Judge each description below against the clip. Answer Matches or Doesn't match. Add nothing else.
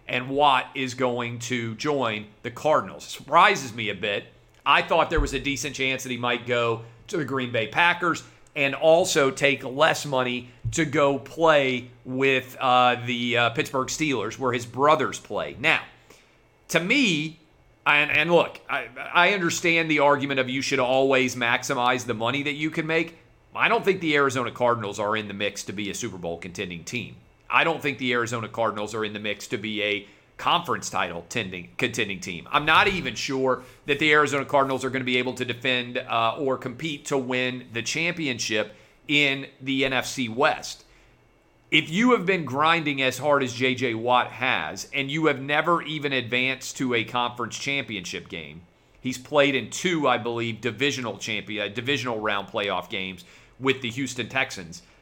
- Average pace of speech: Matches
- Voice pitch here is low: Matches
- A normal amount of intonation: Matches